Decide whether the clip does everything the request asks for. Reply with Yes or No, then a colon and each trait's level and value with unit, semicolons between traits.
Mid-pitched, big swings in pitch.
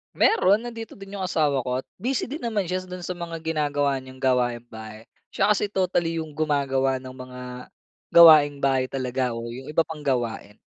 Yes: medium, 145 Hz; wide, 6.0 semitones